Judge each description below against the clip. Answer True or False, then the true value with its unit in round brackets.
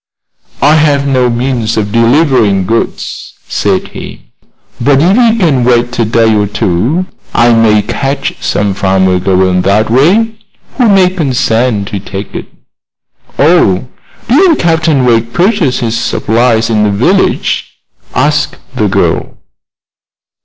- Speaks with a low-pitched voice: True (120 Hz)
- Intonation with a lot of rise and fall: True (6.5 semitones)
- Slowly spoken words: True (130 wpm)